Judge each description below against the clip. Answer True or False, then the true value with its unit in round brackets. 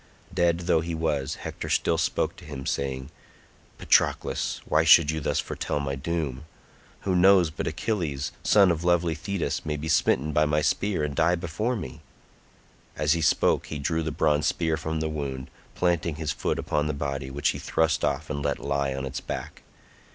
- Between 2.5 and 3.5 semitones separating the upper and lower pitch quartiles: True (2.8 semitones)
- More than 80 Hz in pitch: False (75 Hz)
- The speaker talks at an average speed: True (190 wpm)